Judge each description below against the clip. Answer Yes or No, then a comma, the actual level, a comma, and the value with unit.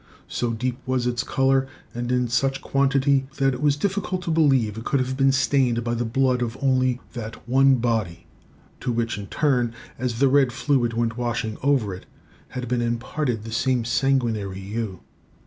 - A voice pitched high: No, low, 125 Hz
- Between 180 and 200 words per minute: Yes, average, 185 wpm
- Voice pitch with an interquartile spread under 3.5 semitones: Yes, narrow, 2.6 semitones